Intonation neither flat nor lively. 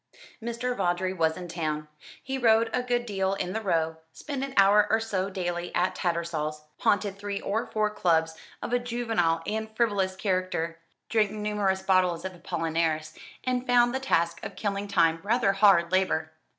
Yes: average, 4.5 semitones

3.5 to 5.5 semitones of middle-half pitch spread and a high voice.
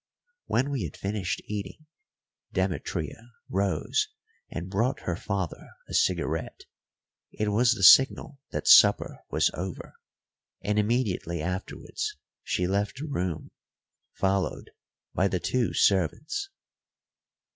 No: average, 4.9 semitones; low, 100 Hz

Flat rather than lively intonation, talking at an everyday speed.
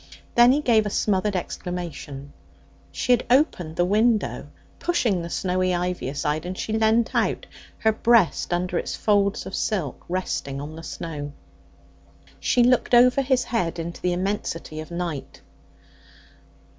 No: average, 4.9 semitones; average, 145 wpm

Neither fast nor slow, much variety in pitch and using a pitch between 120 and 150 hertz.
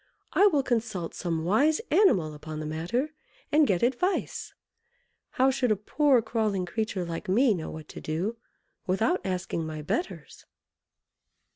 No: average, 145 wpm; wide, 7.8 semitones; high, 215 Hz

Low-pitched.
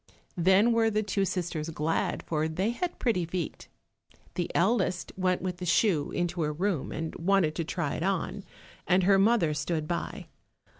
No: medium, 180 Hz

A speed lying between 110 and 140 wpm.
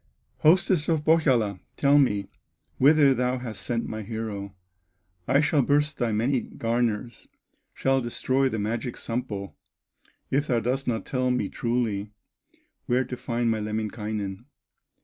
Yes: slow, 135 wpm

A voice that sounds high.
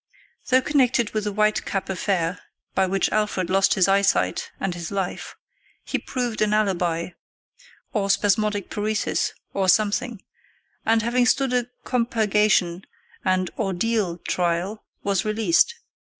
Yes: high, 205 Hz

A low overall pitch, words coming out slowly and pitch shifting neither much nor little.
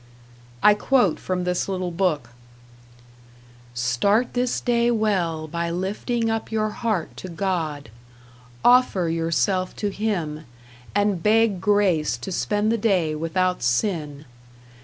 No: medium, 185 Hz; slow, 120 wpm; average, 4.6 semitones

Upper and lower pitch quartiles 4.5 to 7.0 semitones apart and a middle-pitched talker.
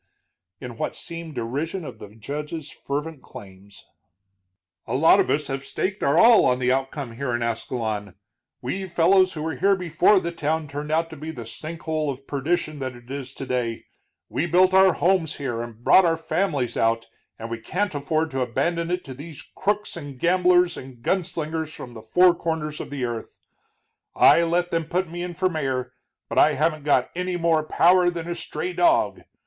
Yes: average, 5.0 semitones; medium, 155 Hz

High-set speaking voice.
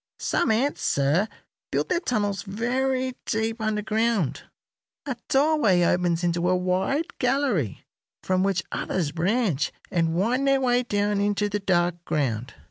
Yes: high, 205 Hz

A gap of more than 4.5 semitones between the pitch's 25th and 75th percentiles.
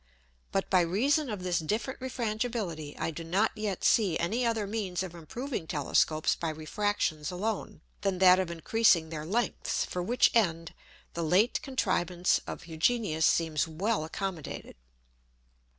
Yes: average, 5.1 semitones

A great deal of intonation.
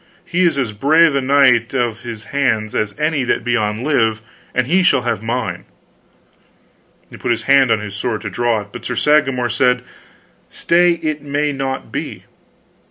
No: average, 4.1 semitones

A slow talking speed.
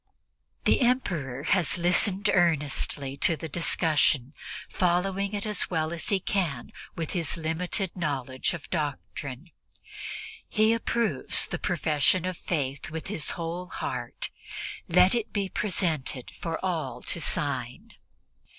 Yes: slow, 130 wpm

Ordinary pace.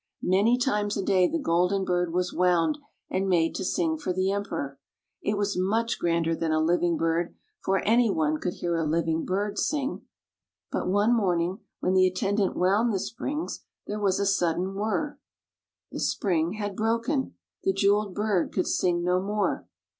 Yes: average, 170 wpm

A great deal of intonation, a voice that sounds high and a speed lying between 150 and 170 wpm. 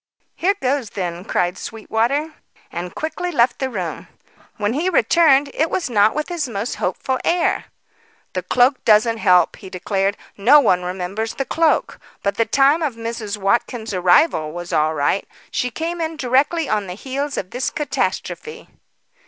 Yes: wide, 6.8 semitones; high, 235 Hz; average, 160 wpm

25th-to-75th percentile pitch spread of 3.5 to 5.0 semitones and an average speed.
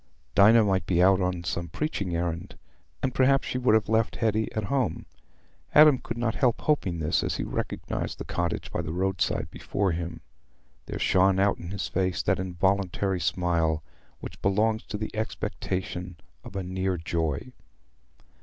Yes: average, 4.0 semitones; average, 170 wpm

